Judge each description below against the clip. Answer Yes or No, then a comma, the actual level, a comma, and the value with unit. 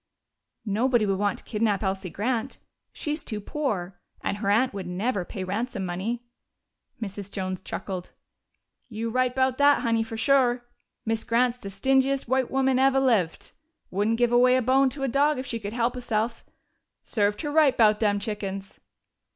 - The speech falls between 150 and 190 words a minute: Yes, average, 170 wpm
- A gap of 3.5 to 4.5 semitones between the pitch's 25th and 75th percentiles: Yes, average, 4.1 semitones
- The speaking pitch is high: Yes, high, 230 Hz